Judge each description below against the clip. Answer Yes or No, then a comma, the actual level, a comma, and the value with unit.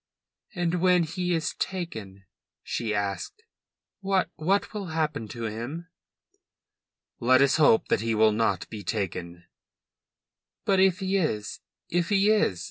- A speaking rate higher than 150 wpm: No, slow, 135 wpm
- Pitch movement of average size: No, wide, 8.9 semitones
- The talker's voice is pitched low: No, medium, 155 Hz